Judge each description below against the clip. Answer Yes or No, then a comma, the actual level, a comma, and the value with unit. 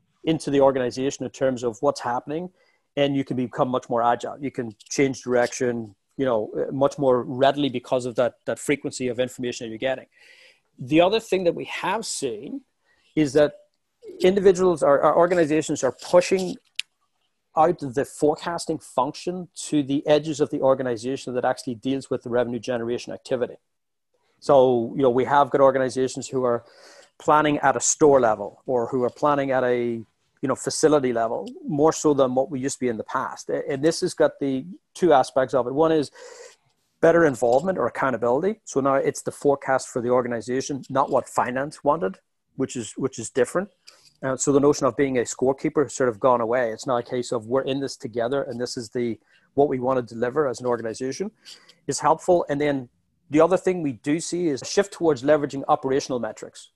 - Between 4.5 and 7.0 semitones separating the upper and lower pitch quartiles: No, average, 3.6 semitones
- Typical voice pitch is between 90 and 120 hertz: No, low, 135 Hz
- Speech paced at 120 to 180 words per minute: No, average, 195 wpm